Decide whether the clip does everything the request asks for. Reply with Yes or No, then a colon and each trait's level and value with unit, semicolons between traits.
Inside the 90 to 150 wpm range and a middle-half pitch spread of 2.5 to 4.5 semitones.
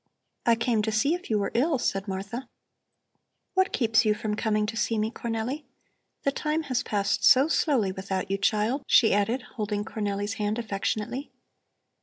No: average, 170 wpm; average, 3.5 semitones